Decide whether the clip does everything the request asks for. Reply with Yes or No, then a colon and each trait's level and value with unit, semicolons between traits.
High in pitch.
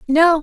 Yes: very high, 315 Hz